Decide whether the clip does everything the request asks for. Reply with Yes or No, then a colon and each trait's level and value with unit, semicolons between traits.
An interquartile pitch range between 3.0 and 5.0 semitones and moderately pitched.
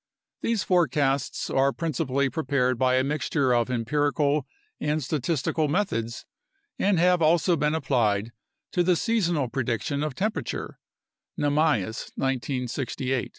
Yes: average, 4.0 semitones; medium, 145 Hz